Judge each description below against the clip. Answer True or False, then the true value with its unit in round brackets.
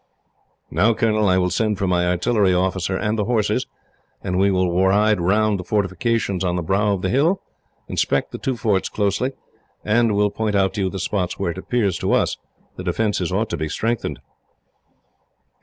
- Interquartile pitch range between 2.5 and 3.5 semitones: True (2.8 semitones)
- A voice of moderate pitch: False (100 Hz)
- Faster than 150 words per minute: True (190 wpm)